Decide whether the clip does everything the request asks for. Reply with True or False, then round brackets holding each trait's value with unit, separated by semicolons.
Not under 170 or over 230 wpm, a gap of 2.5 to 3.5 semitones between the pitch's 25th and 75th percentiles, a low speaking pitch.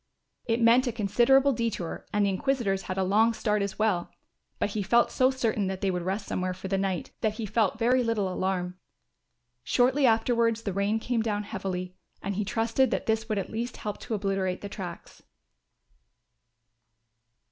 False (180 wpm; 3.2 semitones; 210 Hz)